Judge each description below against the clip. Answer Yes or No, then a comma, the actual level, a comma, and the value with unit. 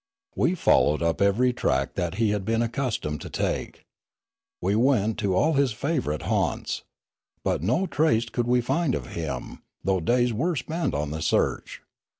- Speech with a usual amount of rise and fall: No, wide, 6.3 semitones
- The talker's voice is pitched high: No, low, 115 Hz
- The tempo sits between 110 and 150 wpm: No, average, 165 wpm